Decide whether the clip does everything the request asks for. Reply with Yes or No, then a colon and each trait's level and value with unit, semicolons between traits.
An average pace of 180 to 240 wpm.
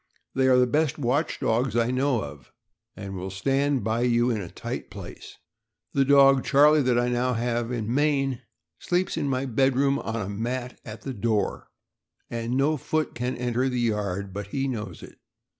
Yes: average, 190 wpm